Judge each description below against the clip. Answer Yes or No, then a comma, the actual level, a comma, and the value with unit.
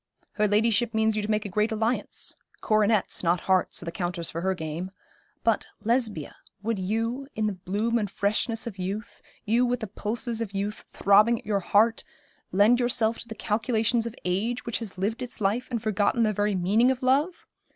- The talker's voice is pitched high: Yes, high, 215 Hz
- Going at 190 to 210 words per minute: Yes, average, 195 wpm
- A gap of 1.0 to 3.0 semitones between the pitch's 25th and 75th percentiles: Yes, average, 2.7 semitones